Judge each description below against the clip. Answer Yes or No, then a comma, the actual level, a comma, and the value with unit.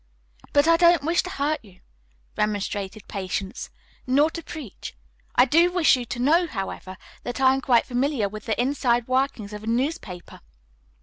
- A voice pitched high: Yes, very high, 255 Hz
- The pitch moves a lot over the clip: Yes, wide, 6.1 semitones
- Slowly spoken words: No, average, 170 wpm